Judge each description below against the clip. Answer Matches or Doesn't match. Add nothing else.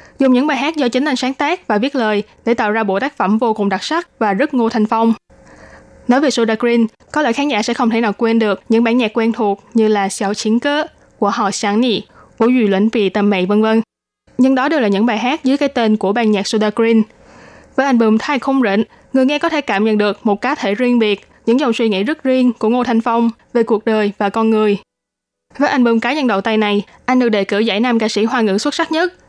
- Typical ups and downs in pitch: Matches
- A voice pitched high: Matches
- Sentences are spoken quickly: Matches